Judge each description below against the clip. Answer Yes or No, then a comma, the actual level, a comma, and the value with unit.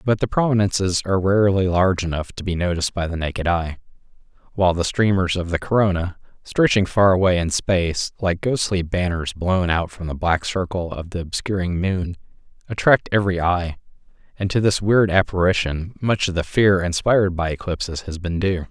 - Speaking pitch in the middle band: No, very low, 90 Hz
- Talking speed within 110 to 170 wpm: No, average, 180 wpm